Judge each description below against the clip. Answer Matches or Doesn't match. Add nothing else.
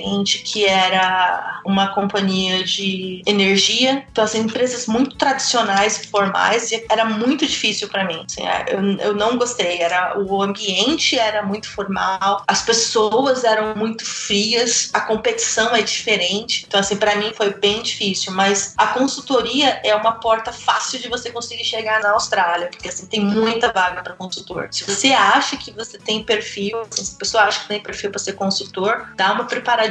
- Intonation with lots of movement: Doesn't match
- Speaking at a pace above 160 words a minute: Matches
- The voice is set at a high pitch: Matches